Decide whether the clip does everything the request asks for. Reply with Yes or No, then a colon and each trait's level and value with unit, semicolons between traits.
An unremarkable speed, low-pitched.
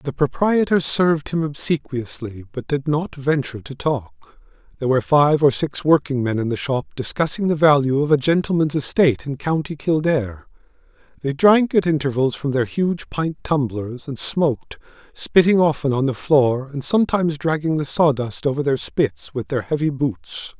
No: average, 170 wpm; medium, 145 Hz